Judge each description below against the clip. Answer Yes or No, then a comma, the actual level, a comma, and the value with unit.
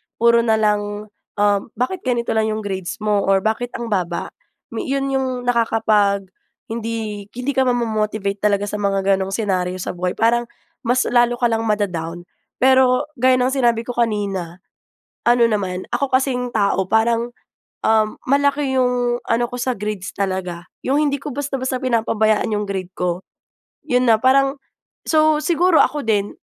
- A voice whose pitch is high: Yes, high, 225 Hz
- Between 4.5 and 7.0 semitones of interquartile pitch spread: No, average, 3.7 semitones